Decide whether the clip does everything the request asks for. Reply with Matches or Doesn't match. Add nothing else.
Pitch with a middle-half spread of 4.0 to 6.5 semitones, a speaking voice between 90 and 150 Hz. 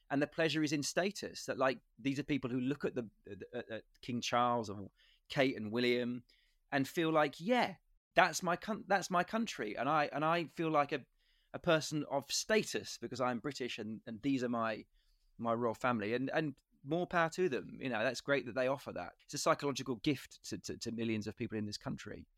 Matches